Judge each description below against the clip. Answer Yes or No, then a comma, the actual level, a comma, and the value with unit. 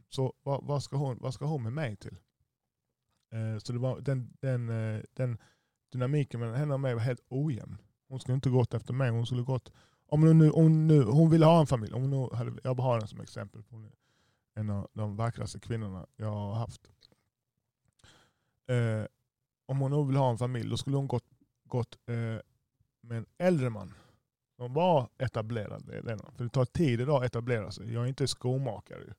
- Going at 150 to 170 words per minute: No, fast, 195 wpm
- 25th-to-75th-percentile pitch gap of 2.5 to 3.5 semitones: Yes, average, 2.9 semitones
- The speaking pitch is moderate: No, low, 125 Hz